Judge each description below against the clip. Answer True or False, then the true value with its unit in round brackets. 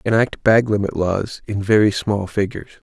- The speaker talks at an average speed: True (165 wpm)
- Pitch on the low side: True (105 Hz)